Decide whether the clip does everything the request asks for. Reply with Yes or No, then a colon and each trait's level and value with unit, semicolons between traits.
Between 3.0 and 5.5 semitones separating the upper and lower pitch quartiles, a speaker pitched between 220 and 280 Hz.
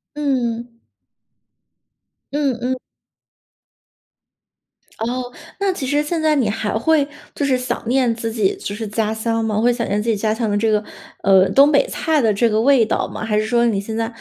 Yes: average, 3.5 semitones; high, 230 Hz